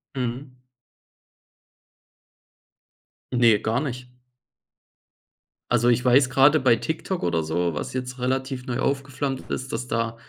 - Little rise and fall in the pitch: Yes, narrow, 2.1 semitones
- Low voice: Yes, low, 125 Hz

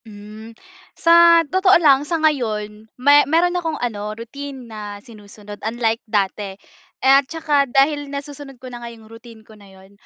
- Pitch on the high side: Yes, high, 240 Hz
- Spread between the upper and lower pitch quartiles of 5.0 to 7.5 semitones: Yes, average, 5.3 semitones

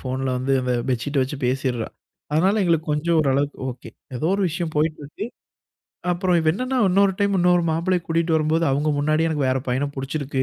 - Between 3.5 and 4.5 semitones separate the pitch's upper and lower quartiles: Yes, average, 4.1 semitones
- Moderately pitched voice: Yes, medium, 155 Hz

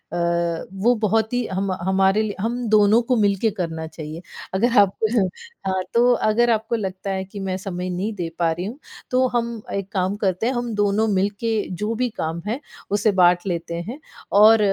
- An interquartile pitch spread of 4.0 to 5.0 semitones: No, average, 3.4 semitones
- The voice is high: Yes, high, 200 Hz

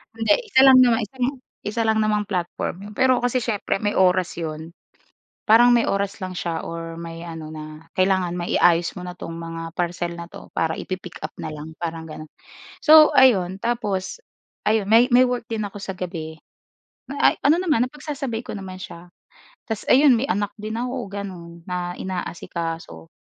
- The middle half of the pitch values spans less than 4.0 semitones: No, average, 5.3 semitones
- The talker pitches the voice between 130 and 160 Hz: No, high, 190 Hz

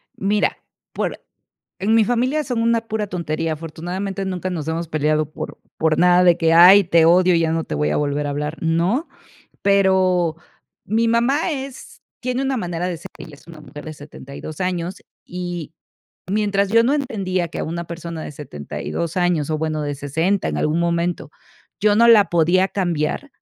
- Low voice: No, medium, 175 Hz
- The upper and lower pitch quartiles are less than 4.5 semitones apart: Yes, average, 4.0 semitones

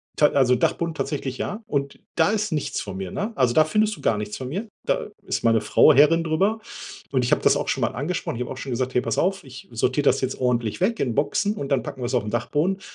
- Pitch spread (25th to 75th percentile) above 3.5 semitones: Yes, wide, 5.5 semitones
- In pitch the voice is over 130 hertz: Yes, medium, 140 Hz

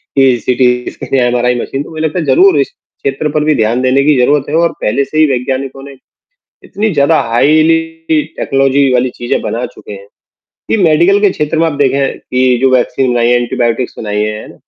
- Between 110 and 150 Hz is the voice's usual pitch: Yes, low, 135 Hz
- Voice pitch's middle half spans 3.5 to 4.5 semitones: Yes, average, 3.8 semitones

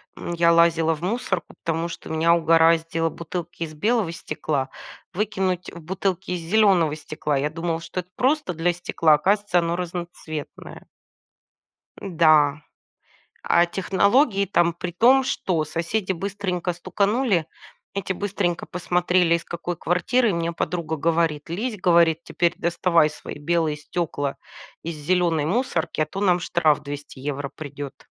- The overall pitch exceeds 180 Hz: No, medium, 170 Hz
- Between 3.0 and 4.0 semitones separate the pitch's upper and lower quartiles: No, narrow, 2.5 semitones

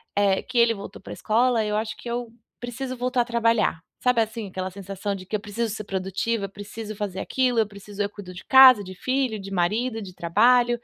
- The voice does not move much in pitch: No, average, 3.4 semitones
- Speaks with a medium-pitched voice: No, high, 215 Hz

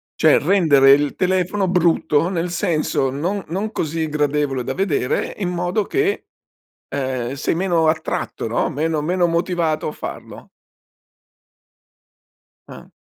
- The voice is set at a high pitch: No, medium, 165 Hz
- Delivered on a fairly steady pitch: No, average, 3.7 semitones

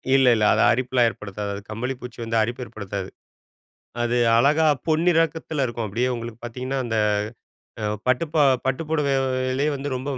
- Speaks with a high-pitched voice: No, low, 125 Hz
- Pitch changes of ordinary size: Yes, average, 3.2 semitones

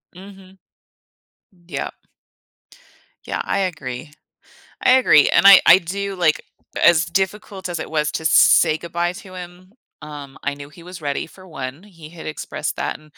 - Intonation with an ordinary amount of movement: Yes, average, 3.6 semitones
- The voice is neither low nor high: Yes, medium, 170 Hz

